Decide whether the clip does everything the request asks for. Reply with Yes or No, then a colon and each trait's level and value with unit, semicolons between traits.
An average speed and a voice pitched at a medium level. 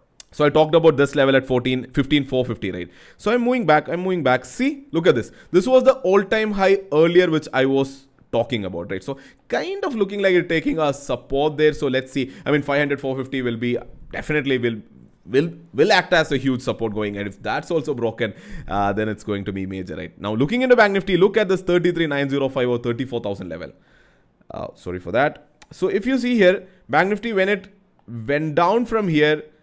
No: fast, 215 wpm; medium, 145 Hz